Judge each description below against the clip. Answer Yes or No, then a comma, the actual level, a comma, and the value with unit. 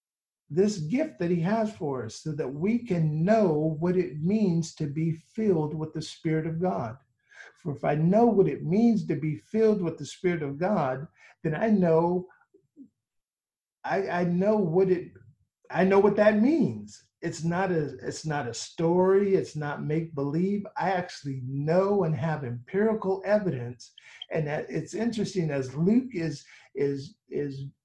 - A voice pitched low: No, medium, 175 Hz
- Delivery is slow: No, average, 170 wpm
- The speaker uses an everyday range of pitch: Yes, average, 4.5 semitones